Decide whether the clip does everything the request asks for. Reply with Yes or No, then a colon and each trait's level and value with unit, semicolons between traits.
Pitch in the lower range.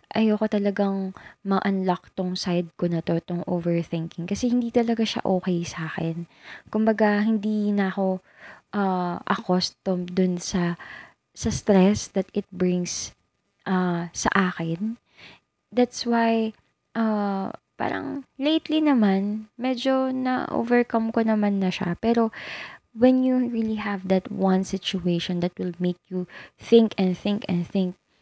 No: high, 195 Hz